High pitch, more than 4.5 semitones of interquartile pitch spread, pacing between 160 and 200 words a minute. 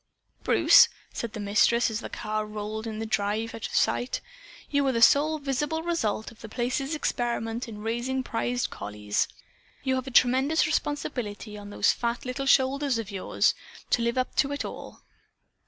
No: high, 235 Hz; average, 3.9 semitones; average, 180 wpm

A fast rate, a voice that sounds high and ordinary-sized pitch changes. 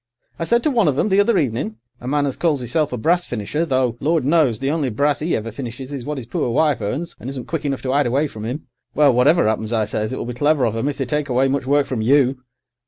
No: fast, 270 wpm; low, 135 Hz; average, 3.7 semitones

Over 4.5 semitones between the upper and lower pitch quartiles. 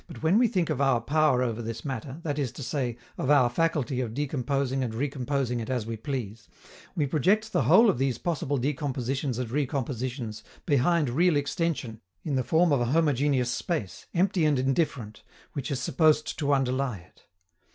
No: average, 3.7 semitones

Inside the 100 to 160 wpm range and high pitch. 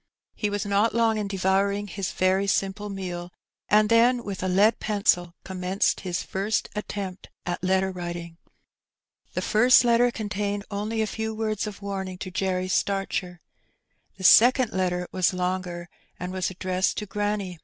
Yes: average, 155 wpm; high, 195 Hz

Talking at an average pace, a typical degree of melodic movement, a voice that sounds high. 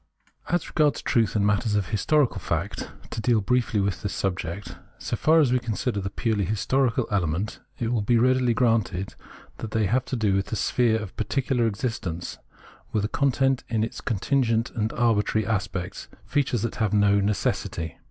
No: average, 180 wpm; average, 3.4 semitones; low, 110 Hz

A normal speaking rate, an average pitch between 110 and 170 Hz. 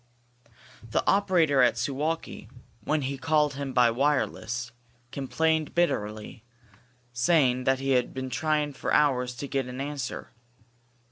No: slow, 130 wpm; low, 135 Hz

